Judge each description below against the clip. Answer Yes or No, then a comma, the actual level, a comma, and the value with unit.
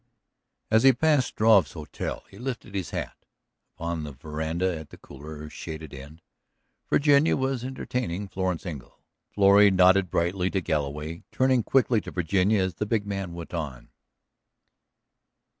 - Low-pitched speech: Yes, very low, 95 Hz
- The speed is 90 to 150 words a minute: Yes, average, 140 wpm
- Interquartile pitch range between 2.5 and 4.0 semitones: No, wide, 5.6 semitones